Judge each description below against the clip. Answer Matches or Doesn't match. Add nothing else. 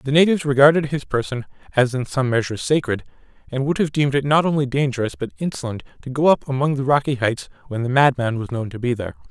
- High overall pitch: Doesn't match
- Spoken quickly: Matches